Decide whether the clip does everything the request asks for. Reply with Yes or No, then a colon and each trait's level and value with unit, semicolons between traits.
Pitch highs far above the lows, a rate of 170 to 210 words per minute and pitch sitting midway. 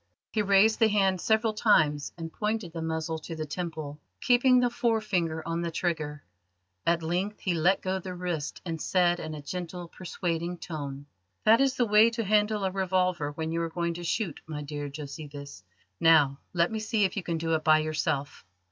No: average, 4.2 semitones; average, 195 wpm; medium, 170 Hz